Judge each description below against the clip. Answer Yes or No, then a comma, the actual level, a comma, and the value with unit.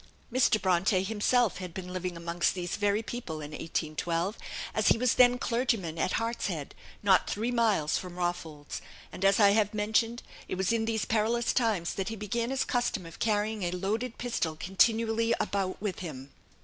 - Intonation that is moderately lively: Yes, average, 4.4 semitones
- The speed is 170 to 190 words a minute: Yes, average, 175 wpm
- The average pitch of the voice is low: No, high, 205 Hz